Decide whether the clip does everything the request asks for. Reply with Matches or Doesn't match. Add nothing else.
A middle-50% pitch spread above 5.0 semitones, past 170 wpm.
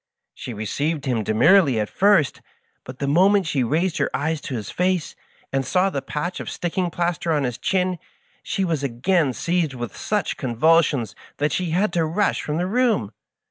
Matches